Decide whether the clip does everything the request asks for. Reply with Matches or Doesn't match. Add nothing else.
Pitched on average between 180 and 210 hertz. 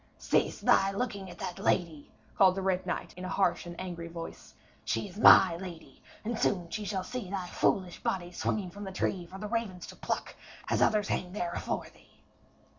Matches